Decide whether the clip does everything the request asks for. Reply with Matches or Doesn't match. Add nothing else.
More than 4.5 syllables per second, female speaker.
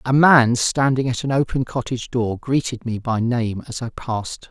Doesn't match